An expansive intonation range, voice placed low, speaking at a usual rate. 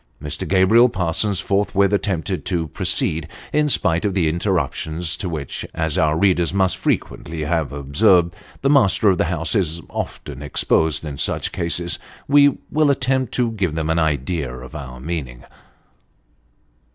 No: average, 4.3 semitones; very low, 85 Hz; average, 150 wpm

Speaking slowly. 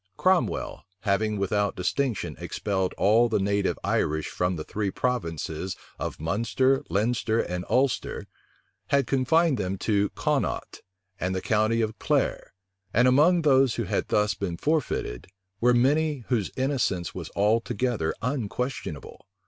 Yes: slow, 130 wpm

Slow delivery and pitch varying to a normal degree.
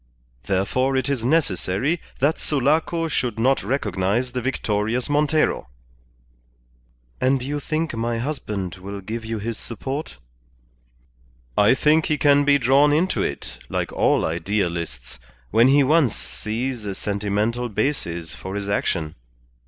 No: slow, 130 wpm; wide, 5.8 semitones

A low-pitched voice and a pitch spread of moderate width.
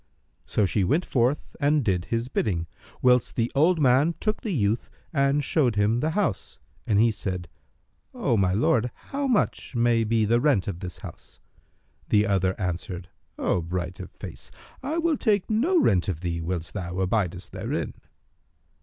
No: low, 115 Hz; wide, 7.9 semitones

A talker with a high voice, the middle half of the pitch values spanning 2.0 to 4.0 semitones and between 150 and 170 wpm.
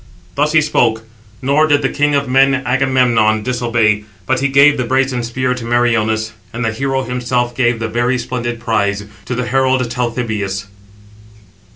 No: low, 125 Hz; narrow, 2.4 semitones; average, 165 wpm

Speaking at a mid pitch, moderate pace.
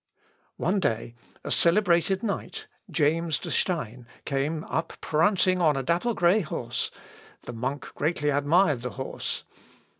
No: medium, 160 Hz; slow, 130 wpm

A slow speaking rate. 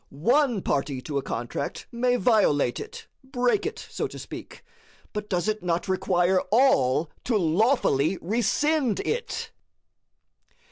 Yes: slow, 130 wpm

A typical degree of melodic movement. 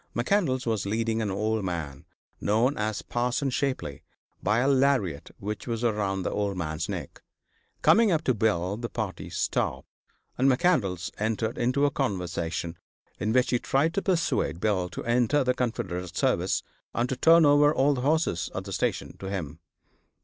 No: wide, 5.7 semitones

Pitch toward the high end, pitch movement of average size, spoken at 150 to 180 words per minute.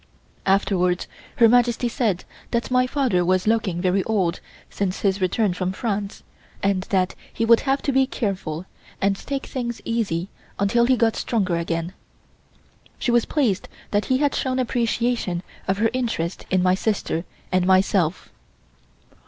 Yes: high, 200 Hz; average, 4.5 semitones; average, 155 wpm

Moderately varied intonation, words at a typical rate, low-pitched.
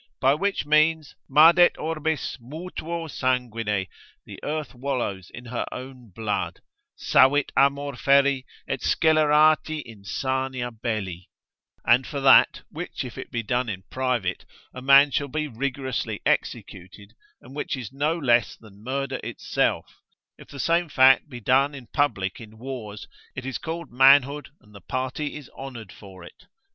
Yes: average, 4.0 semitones; average, 150 wpm; low, 130 Hz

